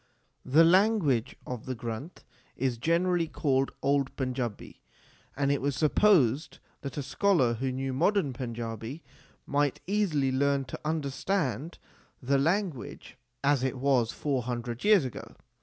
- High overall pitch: No, medium, 140 Hz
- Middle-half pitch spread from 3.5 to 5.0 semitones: Yes, average, 4.1 semitones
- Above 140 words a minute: No, slow, 135 wpm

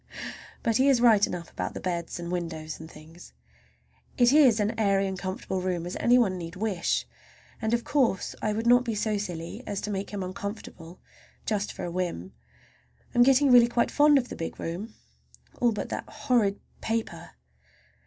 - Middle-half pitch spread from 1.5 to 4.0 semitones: No, average, 4.9 semitones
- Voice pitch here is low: No, high, 205 Hz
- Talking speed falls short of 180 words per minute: No, average, 190 wpm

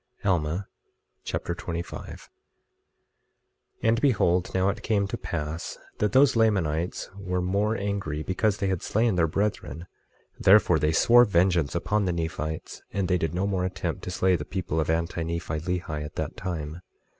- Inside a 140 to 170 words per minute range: Yes, average, 165 wpm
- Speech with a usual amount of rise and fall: Yes, average, 3.5 semitones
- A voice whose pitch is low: Yes, very low, 90 Hz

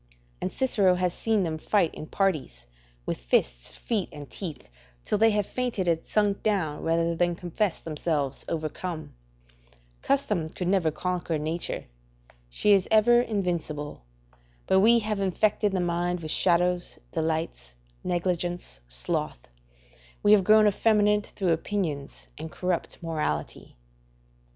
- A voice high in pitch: No, medium, 175 Hz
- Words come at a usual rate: No, slow, 130 wpm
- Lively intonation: No, average, 4.4 semitones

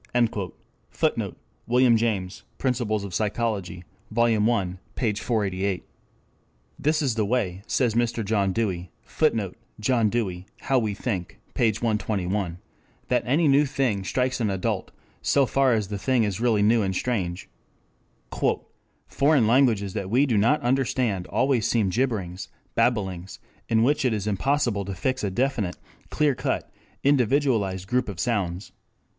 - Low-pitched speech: Yes, low, 110 Hz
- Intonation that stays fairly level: No, average, 4.4 semitones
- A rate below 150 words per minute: Yes, average, 140 wpm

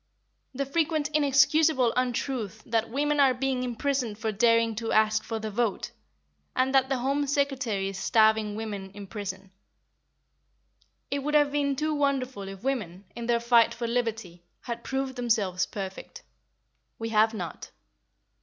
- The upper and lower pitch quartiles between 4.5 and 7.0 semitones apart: No, average, 4.0 semitones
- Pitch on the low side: No, high, 235 Hz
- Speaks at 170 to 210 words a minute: No, average, 150 wpm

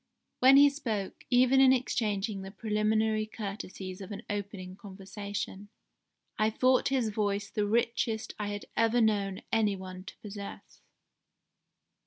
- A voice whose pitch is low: No, high, 210 Hz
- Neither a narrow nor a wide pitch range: No, narrow, 2.3 semitones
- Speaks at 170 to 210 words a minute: No, slow, 135 wpm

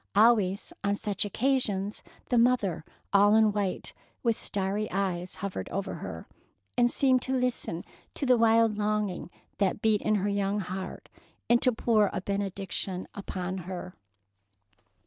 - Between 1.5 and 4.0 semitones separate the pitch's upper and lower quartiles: Yes, average, 2.9 semitones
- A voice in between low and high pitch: No, high, 205 Hz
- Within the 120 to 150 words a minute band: Yes, average, 145 wpm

